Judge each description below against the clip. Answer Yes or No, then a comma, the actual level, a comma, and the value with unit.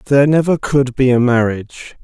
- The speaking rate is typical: Yes, average, 175 wpm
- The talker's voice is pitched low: Yes, low, 130 Hz